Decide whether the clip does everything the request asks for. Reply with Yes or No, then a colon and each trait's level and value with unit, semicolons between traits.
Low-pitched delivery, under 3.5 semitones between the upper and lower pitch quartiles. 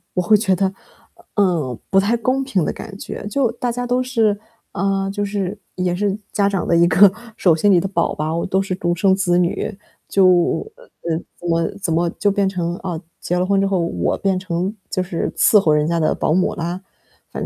No: high, 190 Hz; average, 2.7 semitones